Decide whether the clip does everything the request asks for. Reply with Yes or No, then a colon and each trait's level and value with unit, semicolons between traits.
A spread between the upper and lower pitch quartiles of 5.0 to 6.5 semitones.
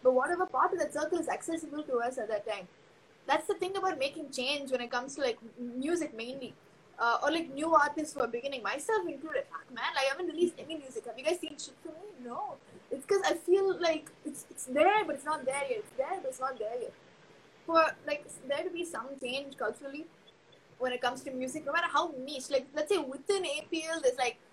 No: average, 4.3 semitones